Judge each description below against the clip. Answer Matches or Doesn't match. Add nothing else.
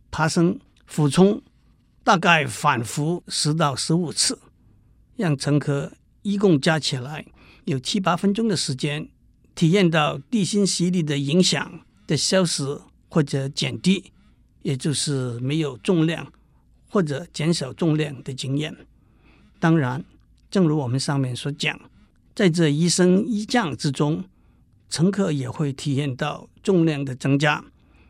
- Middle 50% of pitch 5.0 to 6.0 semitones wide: Doesn't match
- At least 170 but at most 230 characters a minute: Matches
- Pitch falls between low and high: Matches